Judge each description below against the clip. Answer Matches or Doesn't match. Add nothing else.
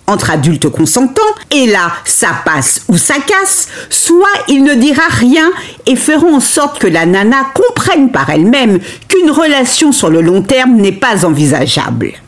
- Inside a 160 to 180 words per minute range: Matches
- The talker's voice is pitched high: Matches